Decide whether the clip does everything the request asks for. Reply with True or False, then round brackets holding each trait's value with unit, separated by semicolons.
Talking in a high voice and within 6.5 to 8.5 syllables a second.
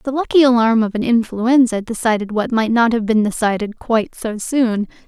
False (230 Hz; 5.2 syllables/s)